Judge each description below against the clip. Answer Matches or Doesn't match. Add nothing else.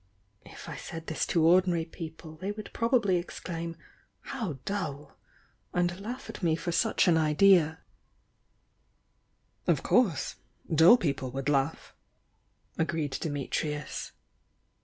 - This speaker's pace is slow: Matches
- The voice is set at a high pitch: Doesn't match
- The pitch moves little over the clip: Doesn't match